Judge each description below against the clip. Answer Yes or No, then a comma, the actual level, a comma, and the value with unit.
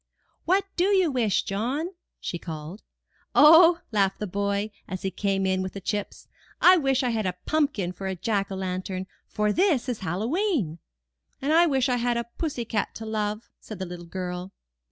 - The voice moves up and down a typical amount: No, wide, 6.4 semitones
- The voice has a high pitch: Yes, high, 210 Hz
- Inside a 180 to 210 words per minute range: Yes, average, 190 wpm